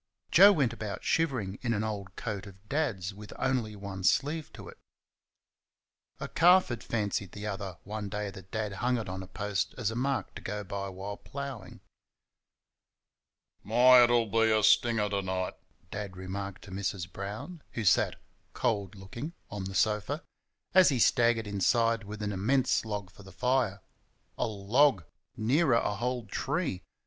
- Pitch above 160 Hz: No, low, 105 Hz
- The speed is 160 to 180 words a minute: Yes, average, 165 wpm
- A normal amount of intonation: Yes, average, 3.7 semitones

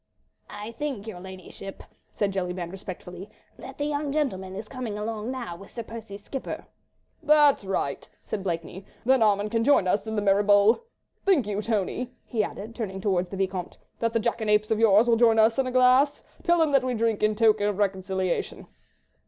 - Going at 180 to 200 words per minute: Yes, average, 190 wpm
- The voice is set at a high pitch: Yes, high, 215 Hz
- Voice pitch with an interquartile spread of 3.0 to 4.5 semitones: Yes, average, 3.7 semitones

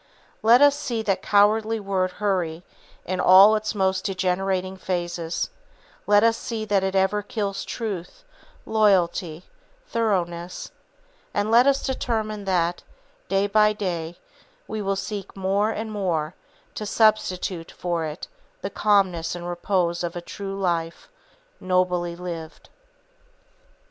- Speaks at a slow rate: Yes, slow, 130 wpm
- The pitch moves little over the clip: No, average, 3.2 semitones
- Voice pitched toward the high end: Yes, high, 195 Hz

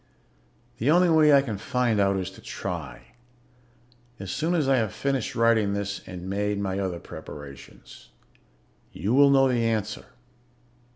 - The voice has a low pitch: Yes, low, 105 Hz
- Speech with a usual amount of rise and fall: No, wide, 5.7 semitones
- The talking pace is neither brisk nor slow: Yes, average, 155 wpm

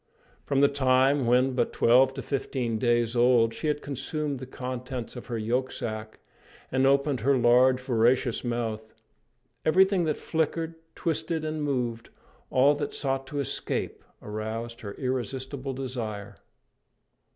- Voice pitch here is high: No, low, 130 Hz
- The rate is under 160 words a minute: Yes, slow, 135 wpm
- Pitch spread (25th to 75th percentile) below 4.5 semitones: Yes, average, 2.8 semitones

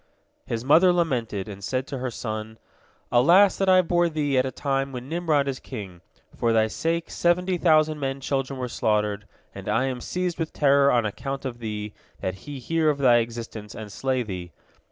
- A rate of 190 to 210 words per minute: Yes, average, 195 wpm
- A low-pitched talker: Yes, low, 130 Hz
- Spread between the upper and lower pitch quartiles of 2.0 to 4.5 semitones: No, wide, 5.5 semitones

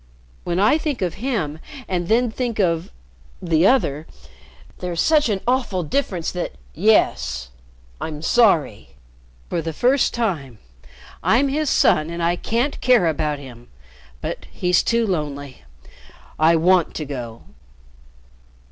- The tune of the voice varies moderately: No, wide, 7.2 semitones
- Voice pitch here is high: No, medium, 175 Hz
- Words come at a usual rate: No, slow, 130 wpm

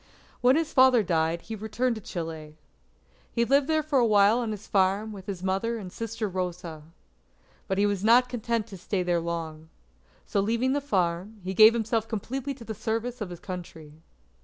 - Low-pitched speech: No, high, 210 Hz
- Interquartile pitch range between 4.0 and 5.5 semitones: Yes, average, 4.5 semitones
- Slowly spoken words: No, average, 185 wpm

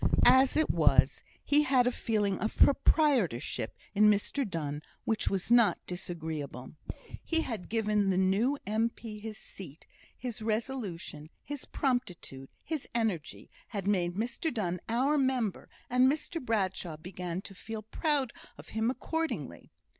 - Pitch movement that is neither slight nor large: No, wide, 5.7 semitones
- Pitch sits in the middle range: No, high, 215 Hz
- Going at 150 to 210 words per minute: No, average, 140 wpm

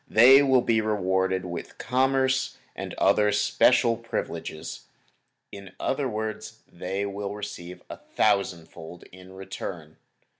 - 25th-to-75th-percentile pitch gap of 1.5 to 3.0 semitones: No, average, 3.8 semitones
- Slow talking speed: Yes, slow, 120 wpm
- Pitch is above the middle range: No, low, 105 Hz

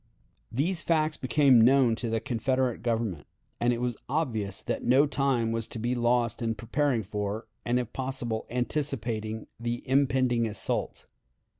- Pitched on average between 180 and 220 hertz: No, low, 120 Hz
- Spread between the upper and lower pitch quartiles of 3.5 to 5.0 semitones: No, average, 2.8 semitones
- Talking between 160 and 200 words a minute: No, average, 150 wpm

